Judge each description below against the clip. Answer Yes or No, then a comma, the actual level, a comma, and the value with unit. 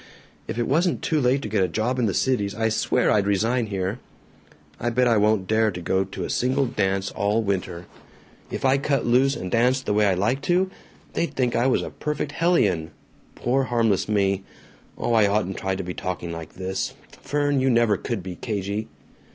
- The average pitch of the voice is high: No, low, 110 Hz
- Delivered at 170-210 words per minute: Yes, average, 200 wpm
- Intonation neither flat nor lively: Yes, average, 4.8 semitones